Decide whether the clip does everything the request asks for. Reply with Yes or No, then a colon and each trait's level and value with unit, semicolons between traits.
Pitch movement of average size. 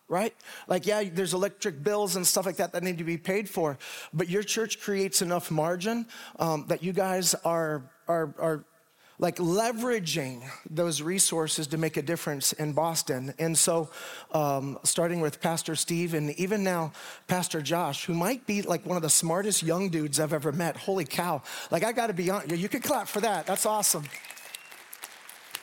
Yes: average, 3.4 semitones